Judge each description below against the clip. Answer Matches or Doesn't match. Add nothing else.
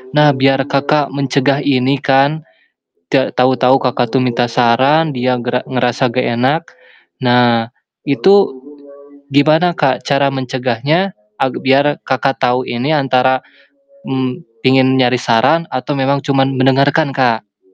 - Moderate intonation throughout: Doesn't match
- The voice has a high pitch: Doesn't match